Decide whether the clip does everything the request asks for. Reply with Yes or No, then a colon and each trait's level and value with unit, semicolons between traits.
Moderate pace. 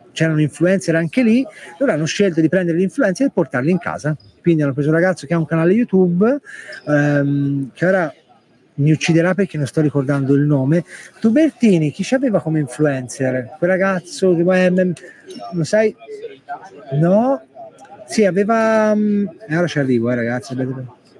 Yes: average, 160 wpm